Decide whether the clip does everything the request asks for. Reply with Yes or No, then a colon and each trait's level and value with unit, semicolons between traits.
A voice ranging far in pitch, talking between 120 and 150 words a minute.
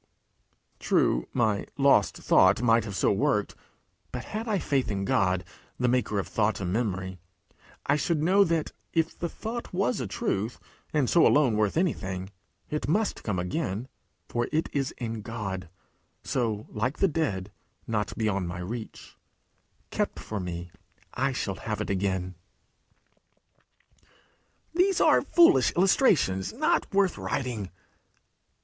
Yes: wide, 8.2 semitones; average, 140 wpm